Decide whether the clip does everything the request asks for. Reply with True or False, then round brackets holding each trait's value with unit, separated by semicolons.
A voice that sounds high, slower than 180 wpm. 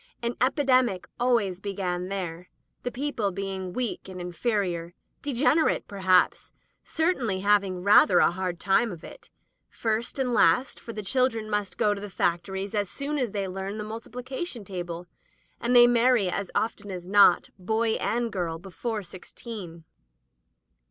True (205 Hz; 160 wpm)